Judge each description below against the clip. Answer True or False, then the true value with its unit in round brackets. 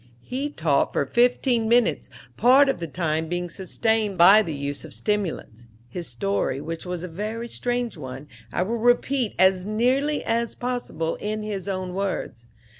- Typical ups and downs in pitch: False (6.0 semitones)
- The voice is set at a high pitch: True (200 Hz)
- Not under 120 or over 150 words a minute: False (165 wpm)